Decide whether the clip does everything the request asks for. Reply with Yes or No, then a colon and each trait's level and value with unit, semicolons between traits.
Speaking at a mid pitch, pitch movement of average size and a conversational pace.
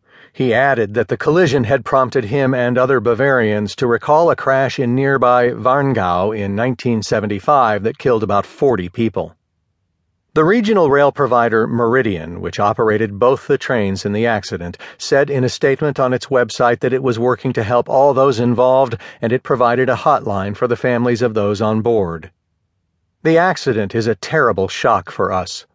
No: low, 120 Hz; average, 4.3 semitones; average, 170 wpm